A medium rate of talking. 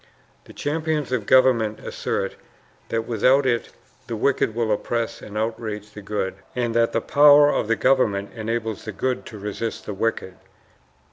Yes: average, 160 wpm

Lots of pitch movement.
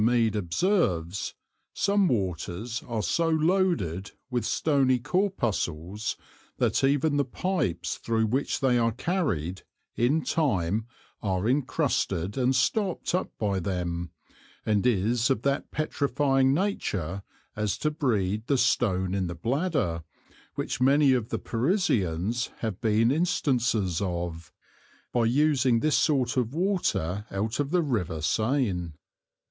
Yes: wide, 6.9 semitones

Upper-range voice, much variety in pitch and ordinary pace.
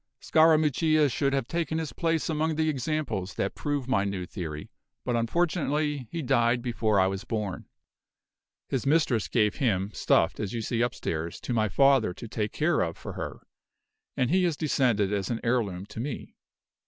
No: low, 125 Hz; wide, 6.4 semitones; average, 175 wpm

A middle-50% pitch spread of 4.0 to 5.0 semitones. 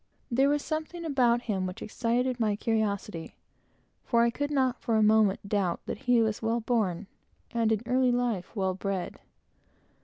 No: average, 3.3 semitones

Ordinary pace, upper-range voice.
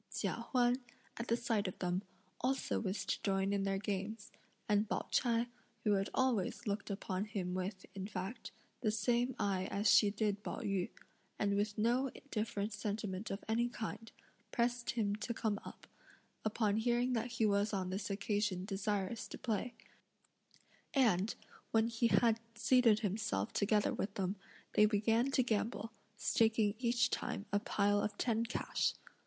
Yes: average, 160 wpm; high, 210 Hz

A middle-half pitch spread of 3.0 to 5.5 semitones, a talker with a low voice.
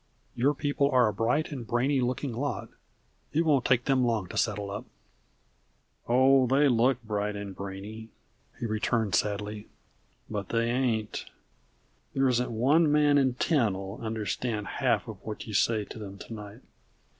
Yes: average, 3.9 semitones; low, 115 Hz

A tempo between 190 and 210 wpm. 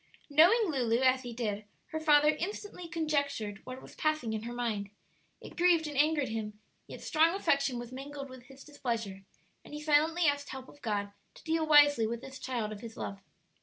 Yes: average, 195 wpm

